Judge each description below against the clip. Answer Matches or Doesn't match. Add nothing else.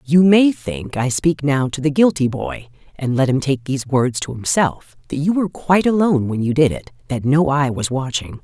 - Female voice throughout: Matches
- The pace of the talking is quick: Matches